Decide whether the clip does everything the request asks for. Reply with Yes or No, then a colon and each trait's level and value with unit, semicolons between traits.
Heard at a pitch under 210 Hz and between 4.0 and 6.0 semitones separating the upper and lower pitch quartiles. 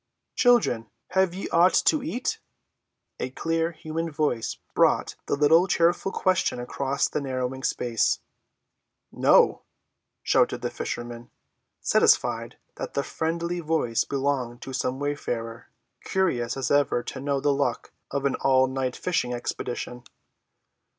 Yes: medium, 140 Hz; average, 5.0 semitones